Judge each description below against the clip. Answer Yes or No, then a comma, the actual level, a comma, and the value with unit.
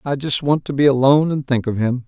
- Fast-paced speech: Yes, fast, 290 wpm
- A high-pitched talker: No, low, 135 Hz